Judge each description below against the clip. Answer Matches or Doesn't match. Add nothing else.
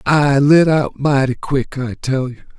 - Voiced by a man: Matches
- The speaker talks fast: Doesn't match